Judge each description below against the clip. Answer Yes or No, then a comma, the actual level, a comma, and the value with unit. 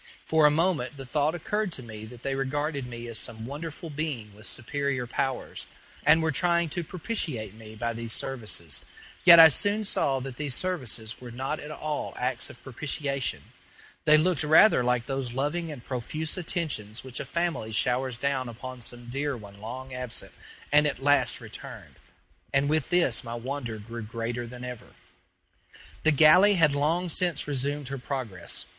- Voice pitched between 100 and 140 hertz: Yes, low, 135 Hz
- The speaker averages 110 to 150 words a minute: No, average, 175 wpm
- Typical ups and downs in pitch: Yes, average, 4.3 semitones